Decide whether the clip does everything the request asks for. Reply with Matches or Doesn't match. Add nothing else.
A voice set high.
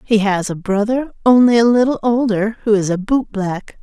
Matches